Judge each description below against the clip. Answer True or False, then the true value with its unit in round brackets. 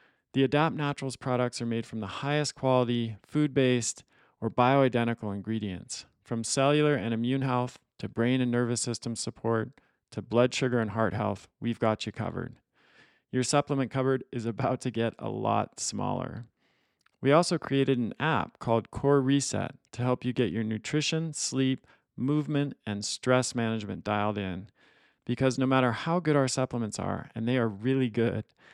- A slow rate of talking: False (165 wpm)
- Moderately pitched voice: False (125 Hz)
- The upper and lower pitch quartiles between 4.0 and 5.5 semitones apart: False (2.8 semitones)